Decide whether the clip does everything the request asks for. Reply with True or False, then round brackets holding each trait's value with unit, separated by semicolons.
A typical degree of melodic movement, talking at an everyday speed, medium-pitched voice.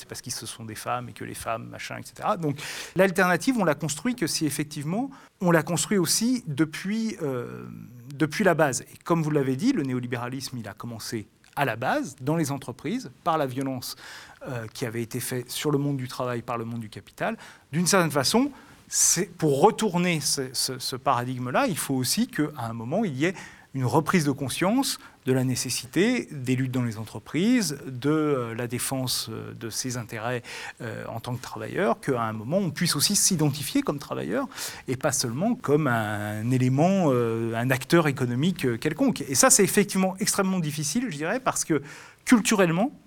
False (6.6 semitones; 190 wpm; 145 Hz)